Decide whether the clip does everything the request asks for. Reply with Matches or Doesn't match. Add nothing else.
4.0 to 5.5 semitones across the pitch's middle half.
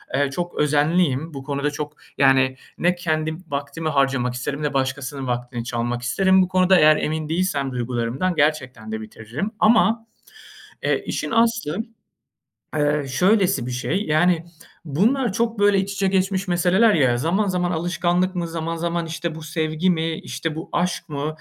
Matches